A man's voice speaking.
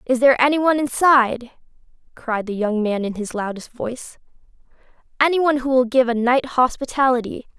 No: female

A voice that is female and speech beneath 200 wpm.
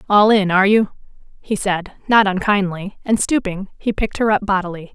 Yes: female; average, 180 wpm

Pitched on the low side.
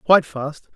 No: medium, 155 Hz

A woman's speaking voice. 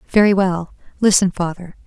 Yes: female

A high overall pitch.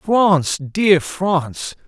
No: medium, 175 Hz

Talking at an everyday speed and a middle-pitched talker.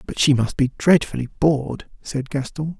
Yes: average, 170 wpm; medium, 145 Hz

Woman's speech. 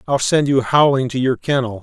No: male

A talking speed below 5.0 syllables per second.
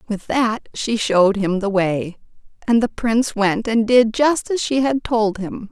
Yes: 4.2 syllables/s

